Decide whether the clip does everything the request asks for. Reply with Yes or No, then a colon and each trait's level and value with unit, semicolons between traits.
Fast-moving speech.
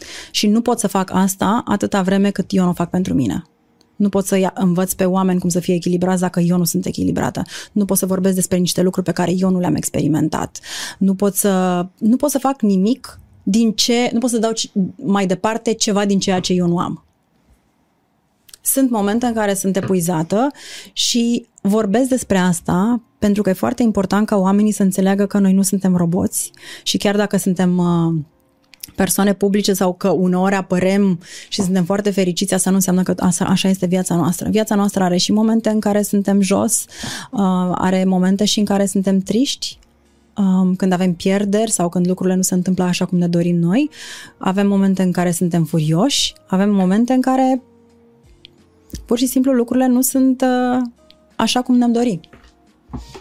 Yes: fast, 185 wpm